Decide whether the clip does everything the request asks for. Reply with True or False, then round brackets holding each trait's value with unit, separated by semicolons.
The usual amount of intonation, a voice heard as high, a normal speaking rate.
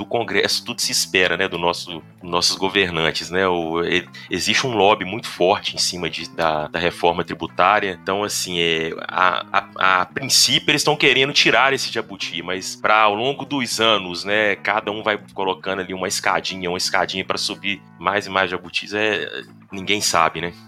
False (3.3 semitones; 95 Hz; 185 wpm)